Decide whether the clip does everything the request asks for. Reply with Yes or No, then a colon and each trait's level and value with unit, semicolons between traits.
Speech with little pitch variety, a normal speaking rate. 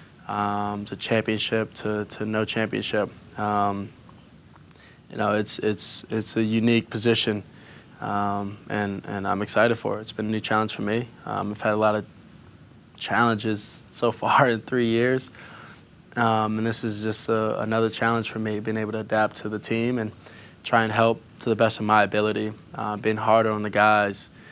Yes: narrow, 1.2 semitones; average, 185 wpm